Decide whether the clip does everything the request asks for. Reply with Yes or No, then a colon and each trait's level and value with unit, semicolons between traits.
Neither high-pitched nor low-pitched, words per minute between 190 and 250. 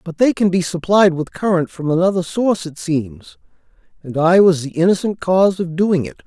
Yes: medium, 175 Hz; average, 200 wpm